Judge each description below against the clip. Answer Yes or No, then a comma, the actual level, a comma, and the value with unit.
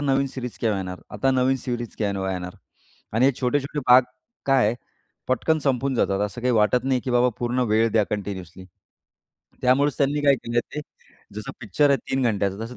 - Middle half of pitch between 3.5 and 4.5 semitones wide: Yes, average, 4.2 semitones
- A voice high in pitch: No, low, 125 Hz